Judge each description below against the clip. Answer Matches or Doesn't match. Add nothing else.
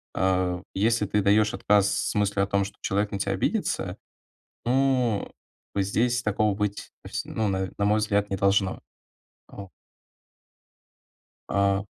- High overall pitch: Doesn't match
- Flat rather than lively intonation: Matches